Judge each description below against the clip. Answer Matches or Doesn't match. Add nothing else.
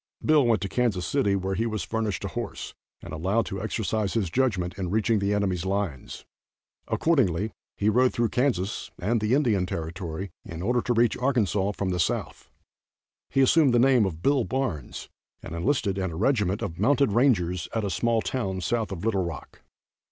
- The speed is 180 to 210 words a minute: Matches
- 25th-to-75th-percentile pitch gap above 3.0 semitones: Matches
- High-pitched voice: Doesn't match